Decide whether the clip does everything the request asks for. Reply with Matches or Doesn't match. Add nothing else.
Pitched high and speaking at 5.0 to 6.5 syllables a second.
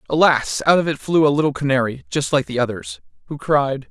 Doesn't match